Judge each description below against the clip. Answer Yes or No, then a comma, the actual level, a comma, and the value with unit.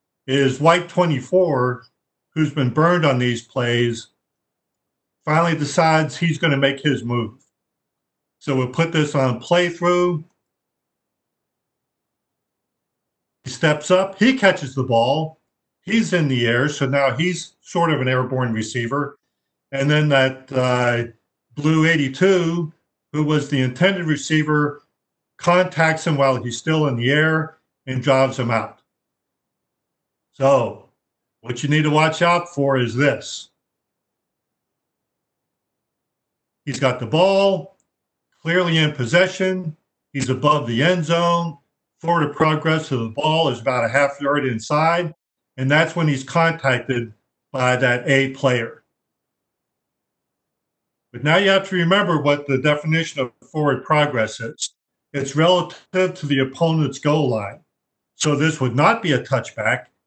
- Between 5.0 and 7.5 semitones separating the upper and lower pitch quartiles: No, average, 4.0 semitones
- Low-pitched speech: No, medium, 150 Hz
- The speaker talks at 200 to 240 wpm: No, slow, 135 wpm